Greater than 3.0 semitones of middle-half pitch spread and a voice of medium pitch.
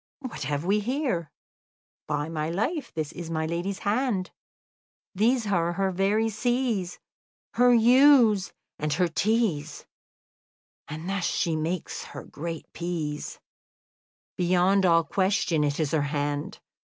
Yes: wide, 5.4 semitones; medium, 180 Hz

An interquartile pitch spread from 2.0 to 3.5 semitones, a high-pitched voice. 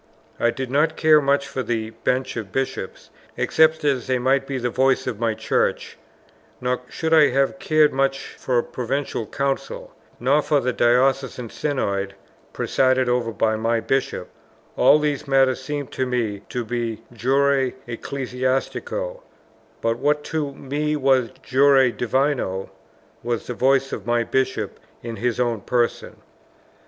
No: narrow, 2.6 semitones; low, 130 Hz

